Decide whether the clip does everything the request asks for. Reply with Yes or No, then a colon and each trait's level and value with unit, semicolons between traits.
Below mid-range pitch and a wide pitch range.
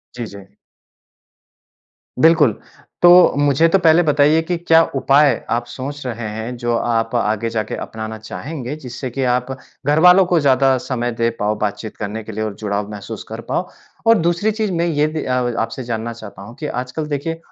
Yes: low, 130 Hz; wide, 5.9 semitones